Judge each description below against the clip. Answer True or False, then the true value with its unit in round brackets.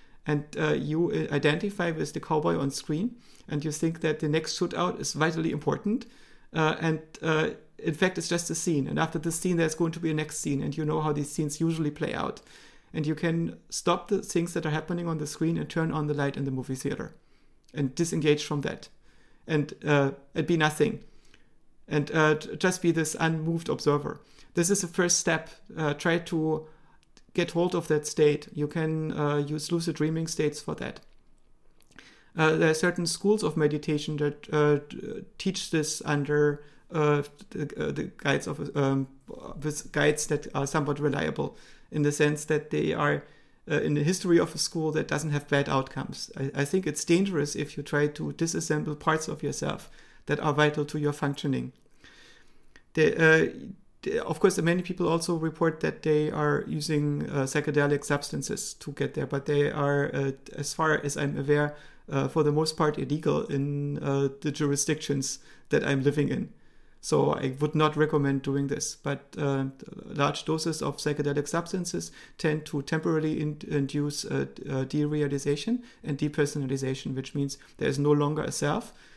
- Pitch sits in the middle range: True (150 Hz)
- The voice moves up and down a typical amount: False (2.1 semitones)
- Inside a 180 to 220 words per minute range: True (185 wpm)